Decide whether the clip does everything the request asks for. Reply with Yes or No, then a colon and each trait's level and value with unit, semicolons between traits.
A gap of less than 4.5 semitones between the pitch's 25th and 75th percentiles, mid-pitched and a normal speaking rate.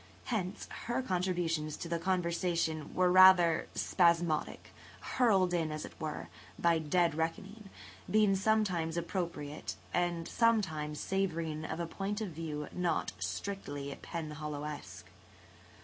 No: average, 3.2 semitones; medium, 170 Hz; slow, 115 wpm